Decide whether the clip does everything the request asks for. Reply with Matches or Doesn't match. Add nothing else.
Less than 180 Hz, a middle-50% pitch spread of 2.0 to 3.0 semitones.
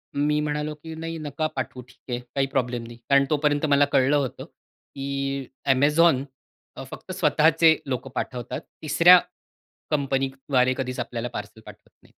Matches